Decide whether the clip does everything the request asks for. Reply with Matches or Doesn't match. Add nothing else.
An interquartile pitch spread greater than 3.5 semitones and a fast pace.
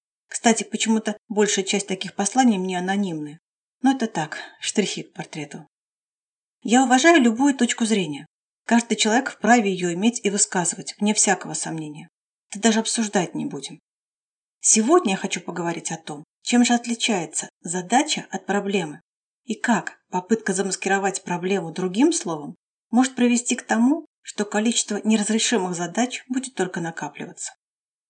Doesn't match